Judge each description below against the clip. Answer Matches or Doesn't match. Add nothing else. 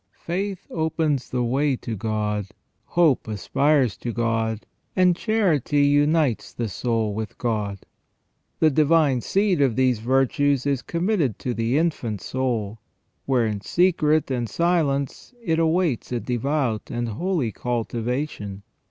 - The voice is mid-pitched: Doesn't match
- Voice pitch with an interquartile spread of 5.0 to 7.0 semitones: Matches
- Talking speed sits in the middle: Doesn't match